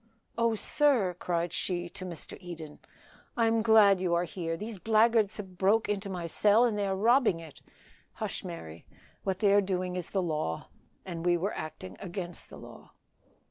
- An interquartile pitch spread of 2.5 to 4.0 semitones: Yes, average, 3.6 semitones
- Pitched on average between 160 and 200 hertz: Yes, medium, 185 Hz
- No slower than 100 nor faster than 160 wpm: No, average, 180 wpm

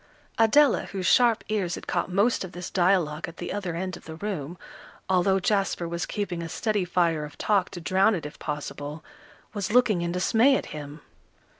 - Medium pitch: Yes, medium, 180 Hz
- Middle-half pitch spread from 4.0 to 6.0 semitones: No, average, 3.4 semitones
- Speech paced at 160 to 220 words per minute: Yes, average, 190 wpm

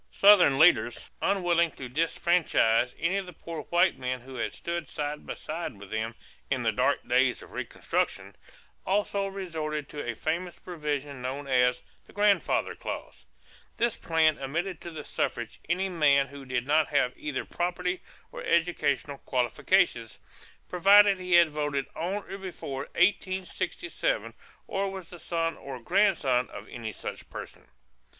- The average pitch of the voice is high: No, medium, 160 Hz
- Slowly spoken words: No, average, 150 wpm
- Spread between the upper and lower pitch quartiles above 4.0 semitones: Yes, average, 5.1 semitones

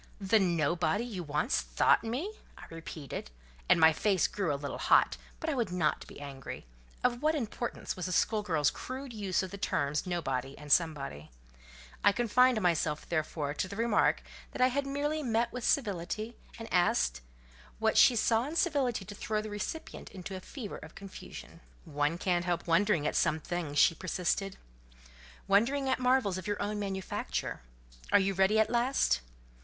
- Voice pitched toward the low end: No, high, 195 Hz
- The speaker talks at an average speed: Yes, average, 175 wpm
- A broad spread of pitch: Yes, wide, 6.2 semitones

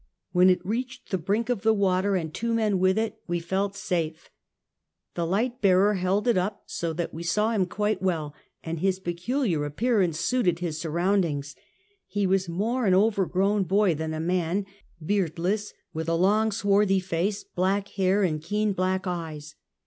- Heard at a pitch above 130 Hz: Yes, high, 190 Hz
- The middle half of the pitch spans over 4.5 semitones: No, average, 3.3 semitones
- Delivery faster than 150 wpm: Yes, average, 175 wpm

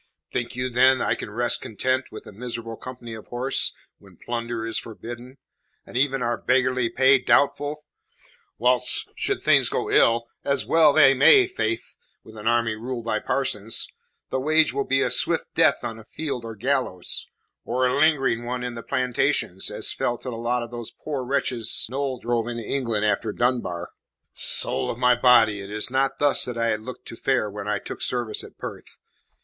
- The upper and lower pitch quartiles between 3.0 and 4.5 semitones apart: No, narrow, 2.4 semitones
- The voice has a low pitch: Yes, low, 120 Hz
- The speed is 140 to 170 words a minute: No, average, 190 wpm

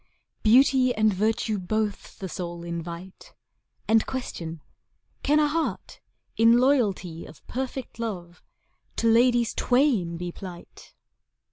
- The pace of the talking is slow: Yes, slow, 115 wpm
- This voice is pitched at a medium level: No, high, 215 Hz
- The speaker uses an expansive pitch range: Yes, wide, 5.9 semitones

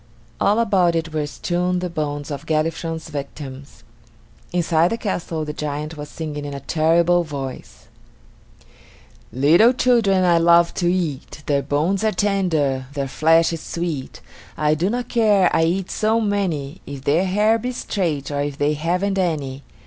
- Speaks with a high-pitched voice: No, medium, 165 Hz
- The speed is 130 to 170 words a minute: Yes, average, 160 wpm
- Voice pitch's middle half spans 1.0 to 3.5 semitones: No, average, 4.1 semitones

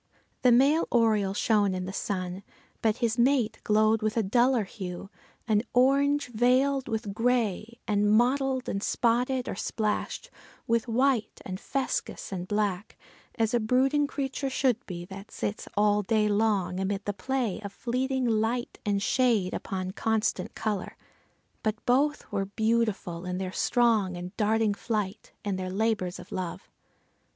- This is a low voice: No, high, 220 Hz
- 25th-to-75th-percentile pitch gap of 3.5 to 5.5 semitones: Yes, average, 3.8 semitones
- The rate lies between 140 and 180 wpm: Yes, average, 150 wpm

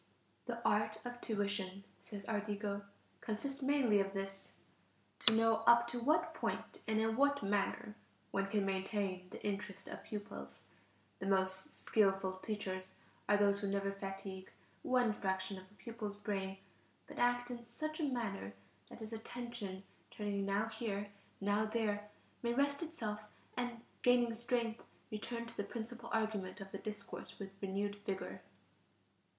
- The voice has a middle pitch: No, high, 210 Hz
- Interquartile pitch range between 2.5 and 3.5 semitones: Yes, average, 3.1 semitones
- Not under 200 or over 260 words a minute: No, average, 150 wpm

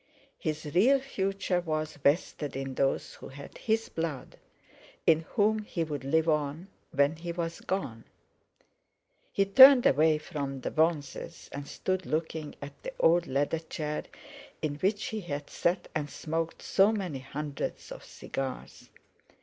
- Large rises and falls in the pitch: No, average, 4.3 semitones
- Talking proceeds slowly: No, average, 145 wpm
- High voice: No, medium, 160 Hz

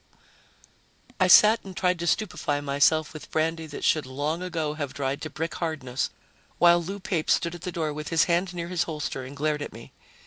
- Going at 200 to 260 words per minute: Yes, fast, 205 wpm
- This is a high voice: No, medium, 160 Hz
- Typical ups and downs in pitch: Yes, average, 3.0 semitones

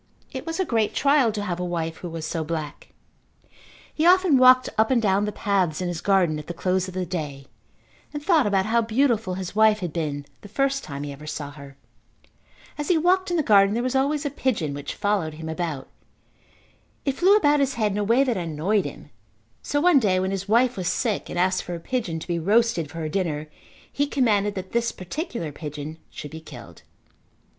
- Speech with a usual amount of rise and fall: No, wide, 7.6 semitones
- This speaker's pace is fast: Yes, fast, 215 wpm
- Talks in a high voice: Yes, high, 200 Hz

